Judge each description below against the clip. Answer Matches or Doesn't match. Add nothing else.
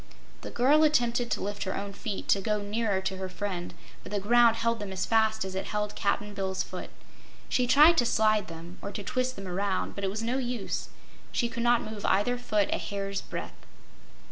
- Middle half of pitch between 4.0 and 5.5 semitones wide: Doesn't match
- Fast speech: Matches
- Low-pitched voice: Doesn't match